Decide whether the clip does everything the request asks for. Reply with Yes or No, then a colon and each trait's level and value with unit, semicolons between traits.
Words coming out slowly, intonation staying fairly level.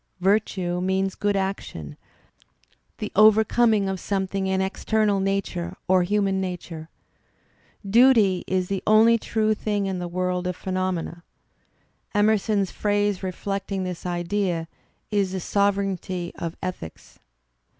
Yes: slow, 125 wpm; narrow, 2.2 semitones